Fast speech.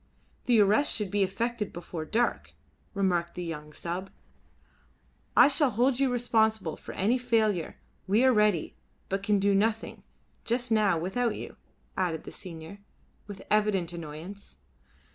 No: average, 145 wpm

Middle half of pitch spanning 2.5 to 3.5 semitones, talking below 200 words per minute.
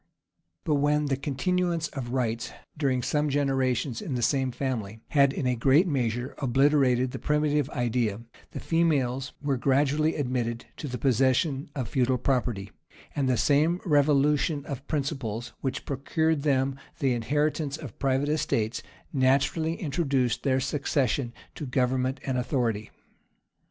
Yes: average, 2.8 semitones; average, 140 wpm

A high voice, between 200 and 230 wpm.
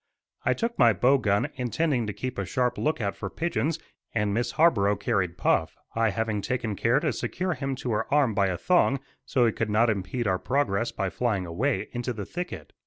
No: low, 115 Hz; fast, 205 wpm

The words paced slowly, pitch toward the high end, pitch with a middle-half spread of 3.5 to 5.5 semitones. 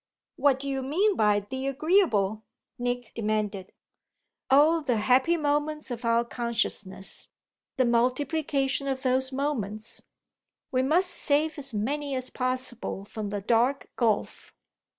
Yes: slow, 130 wpm; very high, 255 Hz; average, 4.1 semitones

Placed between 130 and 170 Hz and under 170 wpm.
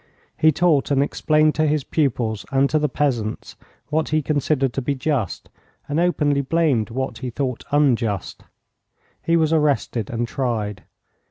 Yes: medium, 140 Hz; average, 155 wpm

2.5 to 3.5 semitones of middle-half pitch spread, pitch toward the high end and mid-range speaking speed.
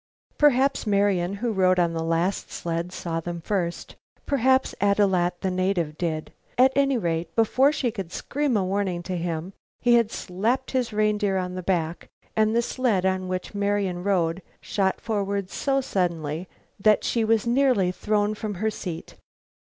No: average, 4.1 semitones; high, 195 Hz; average, 170 wpm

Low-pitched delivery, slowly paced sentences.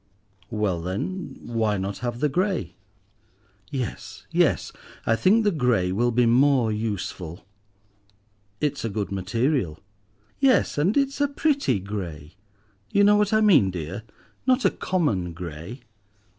Yes: low, 115 Hz; slow, 130 wpm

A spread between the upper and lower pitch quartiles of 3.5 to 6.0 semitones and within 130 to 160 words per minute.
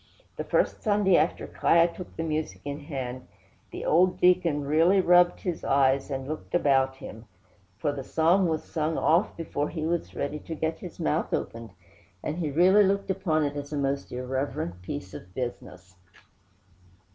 No: average, 4.4 semitones; average, 170 wpm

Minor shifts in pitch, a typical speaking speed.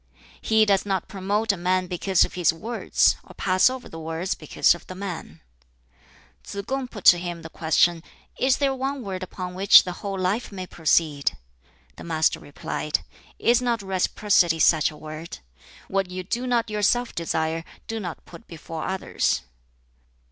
No: average, 4.3 semitones; average, 170 wpm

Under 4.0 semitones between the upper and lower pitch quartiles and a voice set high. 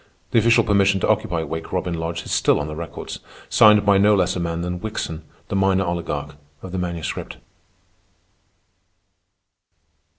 No: average, 2.8 semitones; very low, 90 Hz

